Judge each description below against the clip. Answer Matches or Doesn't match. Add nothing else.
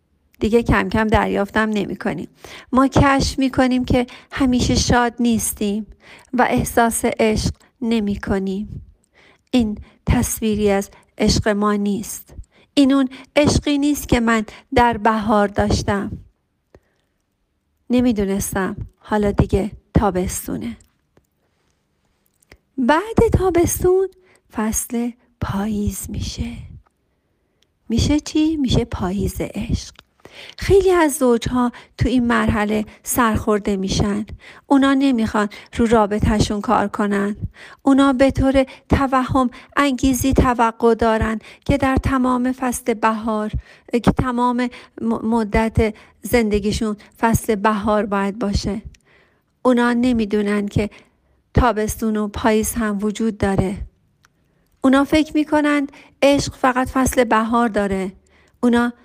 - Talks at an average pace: Doesn't match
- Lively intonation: Doesn't match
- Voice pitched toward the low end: Doesn't match